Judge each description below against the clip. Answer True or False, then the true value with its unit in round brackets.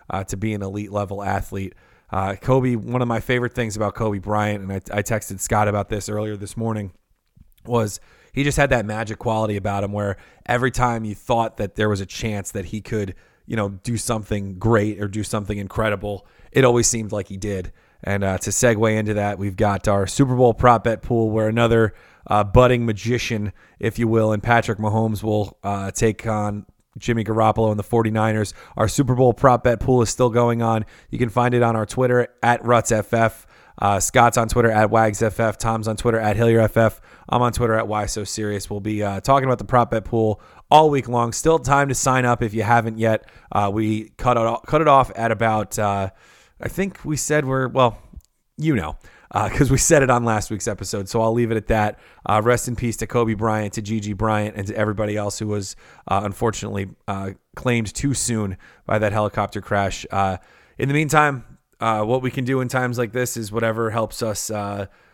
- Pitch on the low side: True (110 Hz)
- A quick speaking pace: True (215 wpm)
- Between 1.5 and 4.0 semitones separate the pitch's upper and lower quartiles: True (2.5 semitones)